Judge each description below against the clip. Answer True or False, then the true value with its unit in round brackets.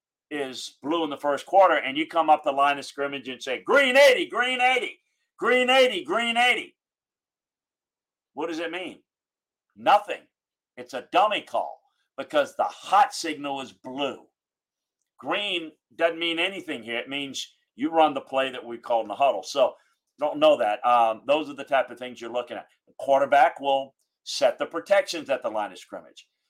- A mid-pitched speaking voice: True (150 Hz)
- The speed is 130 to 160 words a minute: False (185 wpm)